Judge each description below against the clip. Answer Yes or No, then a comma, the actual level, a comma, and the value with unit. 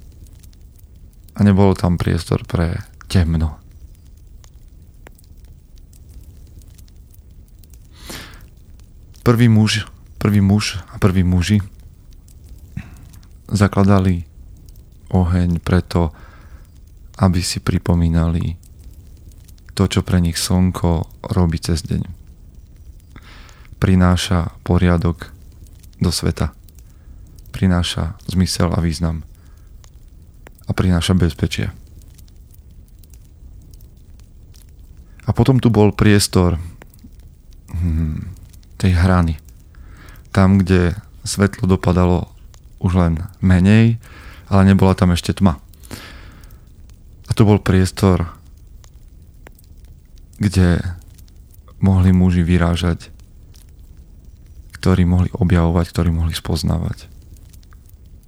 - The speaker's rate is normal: No, slow, 75 wpm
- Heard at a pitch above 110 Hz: No, very low, 90 Hz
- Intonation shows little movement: Yes, narrow, 2.3 semitones